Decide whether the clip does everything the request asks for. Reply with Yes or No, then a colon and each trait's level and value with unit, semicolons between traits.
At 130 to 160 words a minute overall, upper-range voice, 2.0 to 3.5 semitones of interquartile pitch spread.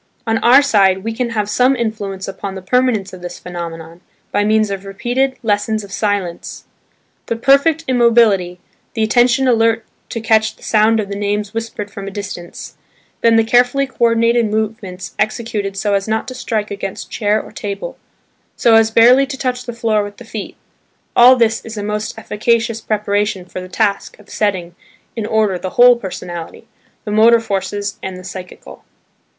No: average, 175 wpm; high, 215 Hz; average, 2.7 semitones